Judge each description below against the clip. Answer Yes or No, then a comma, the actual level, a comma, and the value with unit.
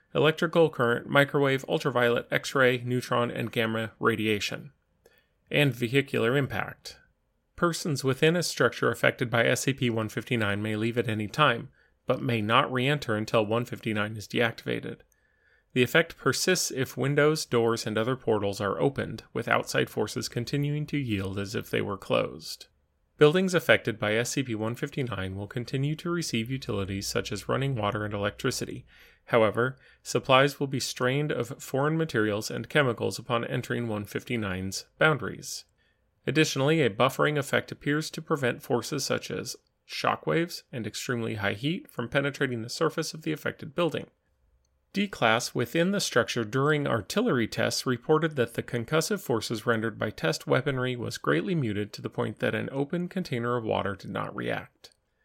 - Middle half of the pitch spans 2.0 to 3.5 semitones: No, average, 4.9 semitones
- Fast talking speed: No, average, 155 wpm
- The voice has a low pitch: Yes, low, 125 Hz